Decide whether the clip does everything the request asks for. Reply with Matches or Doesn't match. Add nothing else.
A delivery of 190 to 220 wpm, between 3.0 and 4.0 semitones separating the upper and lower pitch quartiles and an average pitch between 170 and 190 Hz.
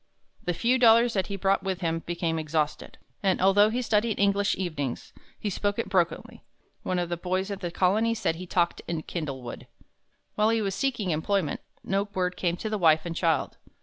Matches